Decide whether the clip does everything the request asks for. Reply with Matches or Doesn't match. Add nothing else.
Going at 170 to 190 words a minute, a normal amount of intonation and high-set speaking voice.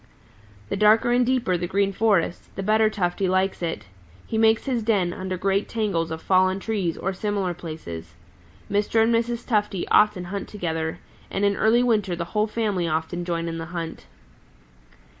Matches